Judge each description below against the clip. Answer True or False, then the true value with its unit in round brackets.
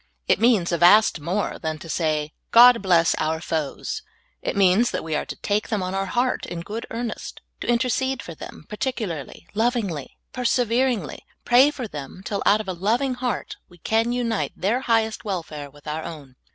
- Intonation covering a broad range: True (6.3 semitones)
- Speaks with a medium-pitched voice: False (205 Hz)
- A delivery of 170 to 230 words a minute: True (190 wpm)